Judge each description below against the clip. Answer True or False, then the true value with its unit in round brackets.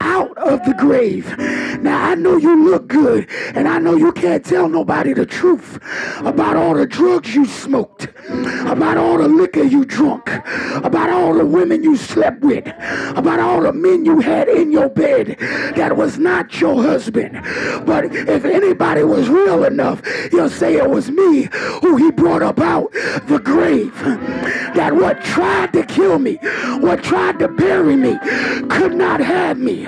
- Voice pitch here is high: True (330 Hz)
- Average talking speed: True (170 wpm)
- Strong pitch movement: False (3.9 semitones)